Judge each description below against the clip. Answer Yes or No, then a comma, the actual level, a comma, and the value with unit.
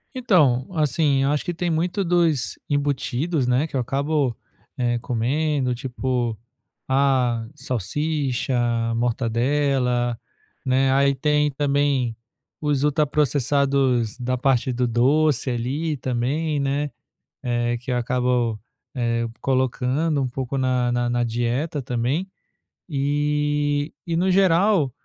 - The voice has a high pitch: No, low, 135 Hz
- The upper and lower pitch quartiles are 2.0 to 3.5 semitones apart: Yes, average, 3.2 semitones